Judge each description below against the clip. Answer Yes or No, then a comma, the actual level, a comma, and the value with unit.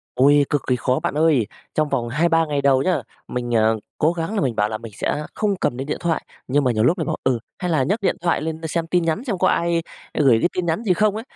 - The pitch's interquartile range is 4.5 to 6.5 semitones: Yes, average, 5.0 semitones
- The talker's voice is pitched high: No, medium, 155 Hz